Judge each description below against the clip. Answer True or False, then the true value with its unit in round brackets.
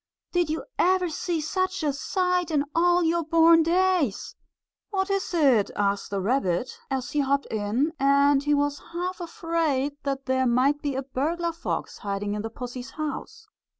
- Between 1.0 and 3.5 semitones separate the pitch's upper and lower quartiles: False (4.7 semitones)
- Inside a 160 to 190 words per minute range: True (170 wpm)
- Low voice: False (290 Hz)